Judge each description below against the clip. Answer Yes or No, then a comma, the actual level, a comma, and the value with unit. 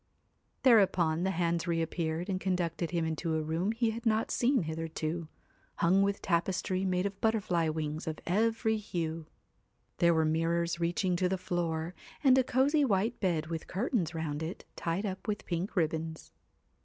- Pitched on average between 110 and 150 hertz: No, medium, 175 Hz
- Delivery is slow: No, average, 165 wpm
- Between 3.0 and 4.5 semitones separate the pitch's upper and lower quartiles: Yes, average, 3.5 semitones